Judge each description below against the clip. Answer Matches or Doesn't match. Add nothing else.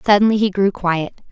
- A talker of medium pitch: Doesn't match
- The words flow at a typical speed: Matches